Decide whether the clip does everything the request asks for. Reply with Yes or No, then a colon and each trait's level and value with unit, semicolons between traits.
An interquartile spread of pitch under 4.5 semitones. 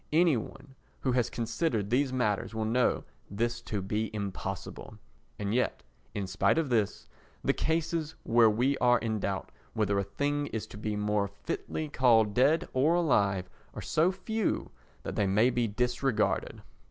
No: average, 5.2 semitones